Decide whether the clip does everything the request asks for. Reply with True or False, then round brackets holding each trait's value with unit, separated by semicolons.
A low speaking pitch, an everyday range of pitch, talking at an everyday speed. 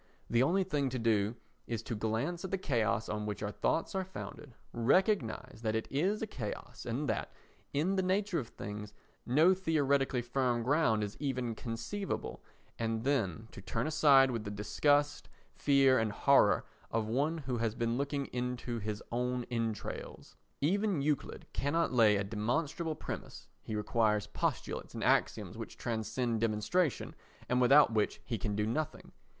True (125 Hz; 5.0 semitones; 165 wpm)